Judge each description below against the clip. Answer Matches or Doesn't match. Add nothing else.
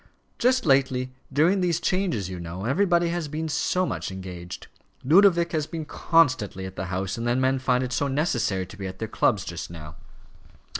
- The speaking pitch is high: Doesn't match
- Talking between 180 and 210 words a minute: Matches